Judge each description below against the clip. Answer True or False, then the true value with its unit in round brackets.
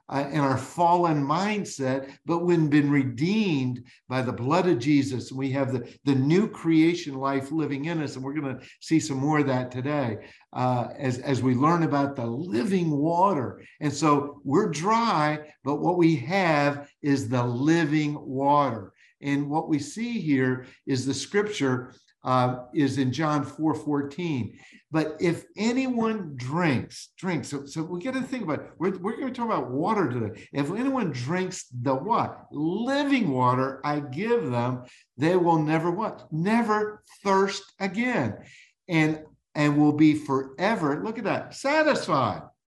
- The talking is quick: False (165 wpm)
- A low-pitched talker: False (150 Hz)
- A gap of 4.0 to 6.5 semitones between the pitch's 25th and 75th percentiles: True (4.5 semitones)